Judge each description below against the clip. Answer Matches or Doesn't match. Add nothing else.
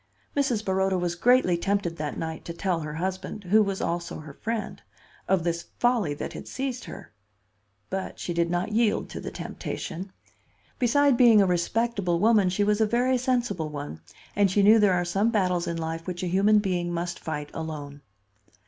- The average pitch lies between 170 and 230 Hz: Matches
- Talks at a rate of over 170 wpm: Matches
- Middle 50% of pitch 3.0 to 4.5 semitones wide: Matches